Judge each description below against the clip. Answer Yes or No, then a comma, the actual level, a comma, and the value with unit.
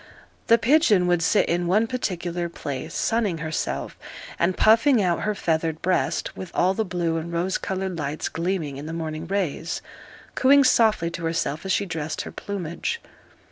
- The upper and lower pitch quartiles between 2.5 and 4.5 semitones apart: Yes, average, 3.7 semitones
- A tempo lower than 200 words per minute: Yes, average, 170 wpm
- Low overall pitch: No, medium, 175 Hz